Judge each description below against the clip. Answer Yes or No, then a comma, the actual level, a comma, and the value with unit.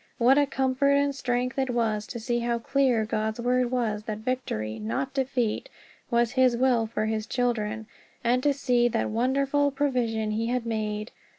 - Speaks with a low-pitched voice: No, high, 240 Hz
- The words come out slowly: No, average, 175 wpm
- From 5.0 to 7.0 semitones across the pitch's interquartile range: No, average, 3.0 semitones